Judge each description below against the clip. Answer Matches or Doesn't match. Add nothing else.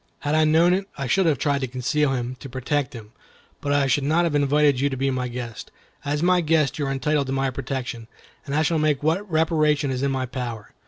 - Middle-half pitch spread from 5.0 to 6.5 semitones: Doesn't match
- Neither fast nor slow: Doesn't match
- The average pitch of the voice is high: Doesn't match